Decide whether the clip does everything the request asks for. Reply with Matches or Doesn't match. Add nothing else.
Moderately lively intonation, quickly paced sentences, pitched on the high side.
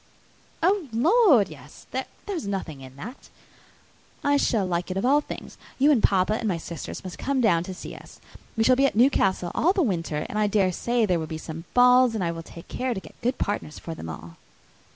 Doesn't match